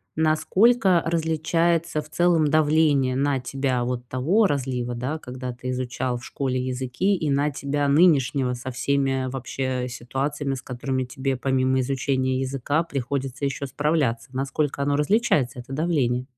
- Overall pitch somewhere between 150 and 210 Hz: No, low, 135 Hz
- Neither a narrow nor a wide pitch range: Yes, average, 3.0 semitones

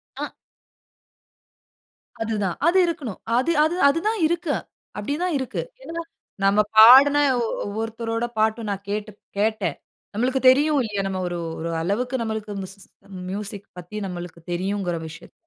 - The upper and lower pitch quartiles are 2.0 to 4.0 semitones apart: No, average, 5.0 semitones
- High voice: Yes, high, 220 Hz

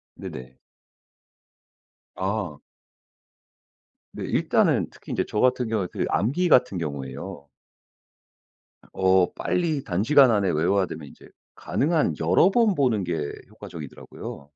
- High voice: No, low, 100 Hz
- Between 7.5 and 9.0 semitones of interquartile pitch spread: Yes, wide, 7.9 semitones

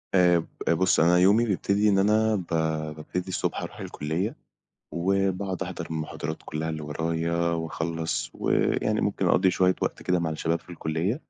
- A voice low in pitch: Yes, very low, 90 Hz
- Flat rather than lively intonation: No, average, 3.0 semitones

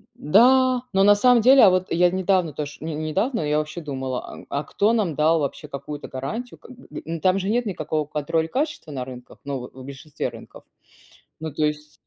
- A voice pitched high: No, medium, 160 Hz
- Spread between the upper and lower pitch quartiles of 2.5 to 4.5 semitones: No, wide, 5.6 semitones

